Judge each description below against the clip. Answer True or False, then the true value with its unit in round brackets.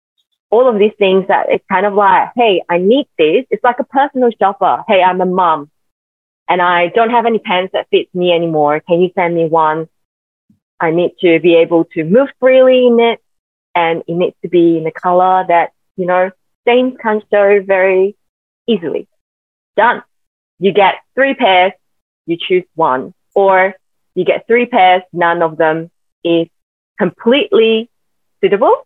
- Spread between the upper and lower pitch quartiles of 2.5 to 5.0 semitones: False (5.6 semitones)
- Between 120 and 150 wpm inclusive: False (170 wpm)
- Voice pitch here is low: False (185 Hz)